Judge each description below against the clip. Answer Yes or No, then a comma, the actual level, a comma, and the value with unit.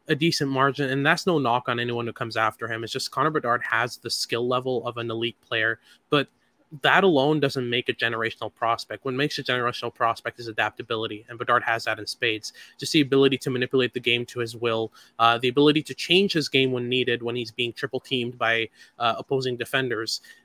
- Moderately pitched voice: No, low, 120 Hz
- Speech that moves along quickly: Yes, fast, 215 wpm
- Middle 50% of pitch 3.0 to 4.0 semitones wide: No, narrow, 2.5 semitones